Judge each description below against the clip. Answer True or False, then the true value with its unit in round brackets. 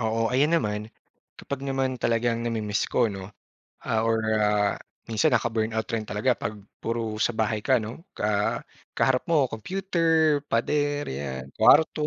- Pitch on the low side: True (115 Hz)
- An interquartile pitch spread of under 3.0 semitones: False (3.9 semitones)